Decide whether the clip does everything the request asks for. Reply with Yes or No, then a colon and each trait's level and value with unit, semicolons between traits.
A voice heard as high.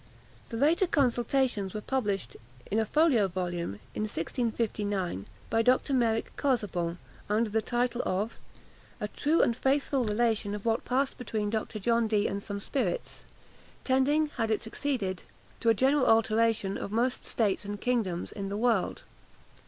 Yes: high, 225 Hz